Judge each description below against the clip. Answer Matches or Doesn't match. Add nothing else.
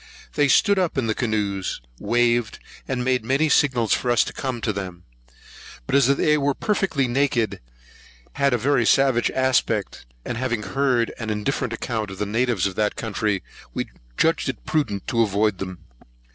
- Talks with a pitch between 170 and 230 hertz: Doesn't match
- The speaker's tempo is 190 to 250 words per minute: Doesn't match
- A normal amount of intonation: Matches